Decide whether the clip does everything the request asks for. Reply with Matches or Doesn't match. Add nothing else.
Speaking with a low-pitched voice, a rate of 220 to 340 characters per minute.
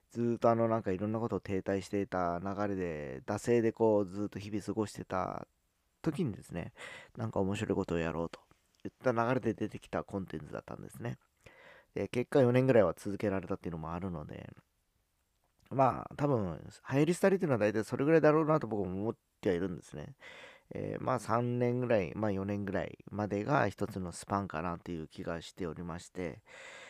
Doesn't match